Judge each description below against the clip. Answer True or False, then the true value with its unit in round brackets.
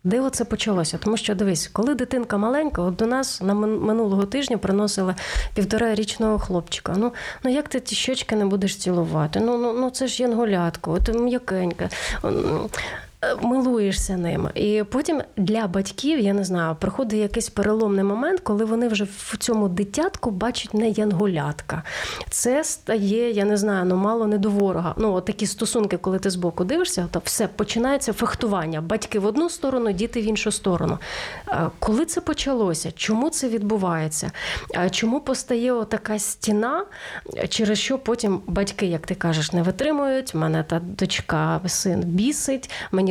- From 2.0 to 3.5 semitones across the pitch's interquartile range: False (3.9 semitones)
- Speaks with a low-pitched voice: False (215 Hz)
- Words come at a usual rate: False (160 wpm)